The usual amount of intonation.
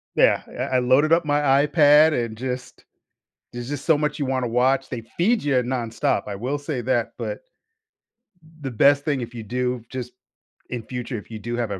Yes: average, 3.3 semitones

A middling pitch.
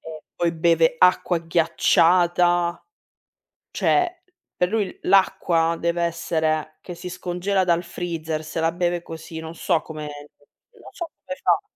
Yes: medium, 170 Hz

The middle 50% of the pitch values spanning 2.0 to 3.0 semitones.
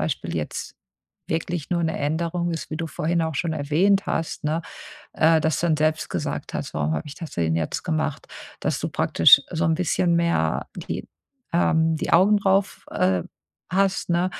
Yes: narrow, 2.4 semitones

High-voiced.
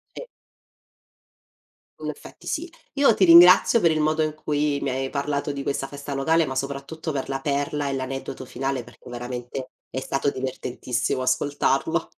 No: medium, 140 Hz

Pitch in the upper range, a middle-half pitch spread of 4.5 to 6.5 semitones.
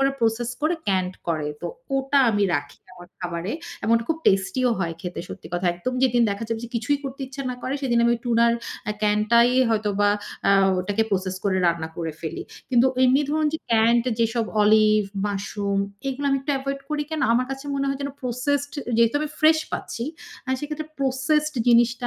Yes: high, 235 Hz; average, 5.1 semitones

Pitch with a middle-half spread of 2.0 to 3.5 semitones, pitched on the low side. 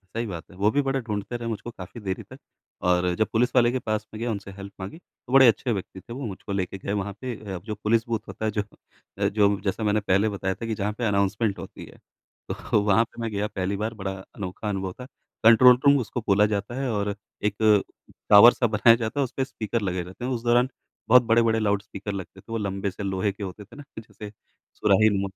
Yes: average, 2.9 semitones; low, 105 Hz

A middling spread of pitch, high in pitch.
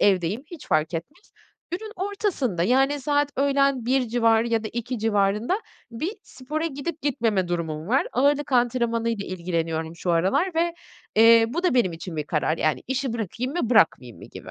No: wide, 7.3 semitones; high, 235 Hz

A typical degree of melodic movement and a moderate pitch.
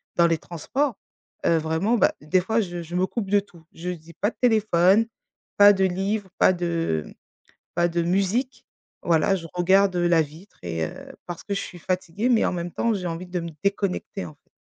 Yes: average, 3.0 semitones; medium, 180 Hz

